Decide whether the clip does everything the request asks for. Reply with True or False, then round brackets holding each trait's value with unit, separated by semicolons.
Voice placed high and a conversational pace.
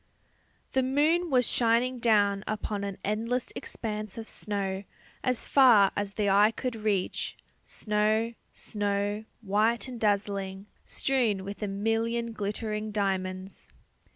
False (210 Hz; 125 wpm)